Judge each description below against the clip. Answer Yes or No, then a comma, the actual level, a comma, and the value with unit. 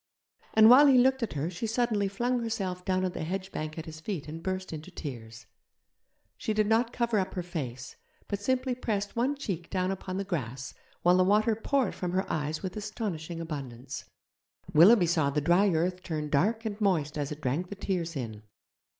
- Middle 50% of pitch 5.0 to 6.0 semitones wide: Yes, wide, 5.5 semitones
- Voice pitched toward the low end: No, medium, 185 Hz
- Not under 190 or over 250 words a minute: Yes, average, 200 wpm